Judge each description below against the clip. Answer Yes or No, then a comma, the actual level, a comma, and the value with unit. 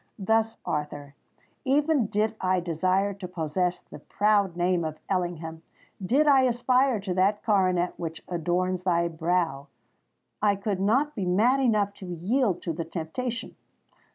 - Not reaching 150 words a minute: Yes, slow, 135 wpm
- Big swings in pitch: No, average, 4.2 semitones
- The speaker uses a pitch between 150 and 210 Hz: Yes, medium, 185 Hz